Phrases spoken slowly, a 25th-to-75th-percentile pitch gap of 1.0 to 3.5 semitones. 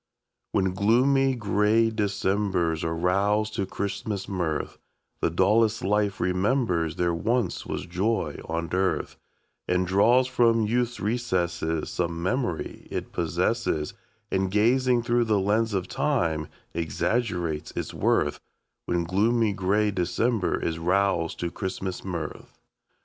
No: slow, 120 wpm; average, 4.5 semitones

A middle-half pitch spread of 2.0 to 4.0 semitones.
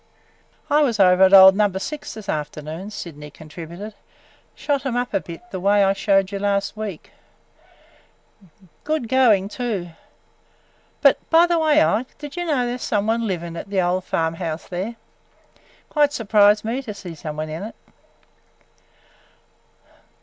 No: average, 5.2 semitones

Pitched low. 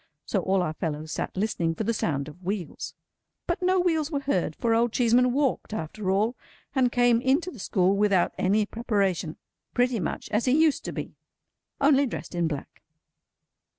No: high, 220 Hz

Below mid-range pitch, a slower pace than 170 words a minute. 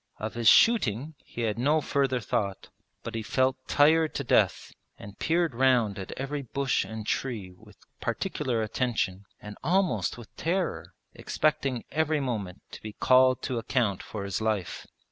Yes: low, 125 Hz; average, 160 wpm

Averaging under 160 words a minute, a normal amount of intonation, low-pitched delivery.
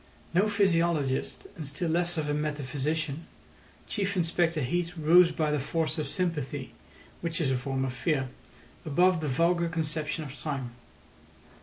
No: average, 150 wpm; average, 3.2 semitones; medium, 155 Hz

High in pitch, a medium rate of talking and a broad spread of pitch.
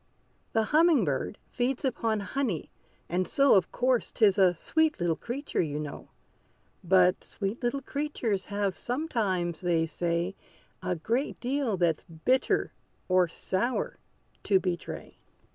No: high, 200 Hz; slow, 130 wpm; wide, 6.2 semitones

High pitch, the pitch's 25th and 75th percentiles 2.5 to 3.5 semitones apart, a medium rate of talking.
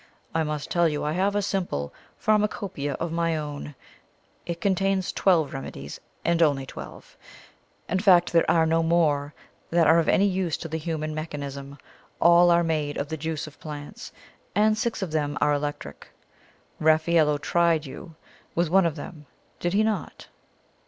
No: medium, 160 Hz; average, 2.9 semitones; average, 165 wpm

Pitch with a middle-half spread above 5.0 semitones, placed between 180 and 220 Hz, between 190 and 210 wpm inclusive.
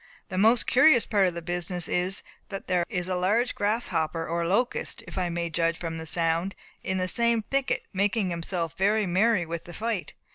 No: average, 3.9 semitones; medium, 185 Hz; average, 195 wpm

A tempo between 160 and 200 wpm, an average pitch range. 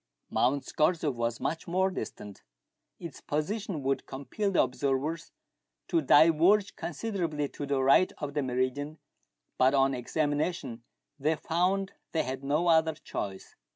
No: slow, 135 wpm; average, 4.3 semitones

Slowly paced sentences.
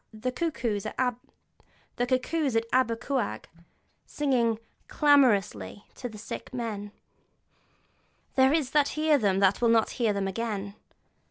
Yes: slow, 115 wpm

